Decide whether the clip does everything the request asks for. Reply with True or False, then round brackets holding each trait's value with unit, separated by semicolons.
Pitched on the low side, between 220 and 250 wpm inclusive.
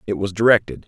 False (105 Hz; 205 wpm)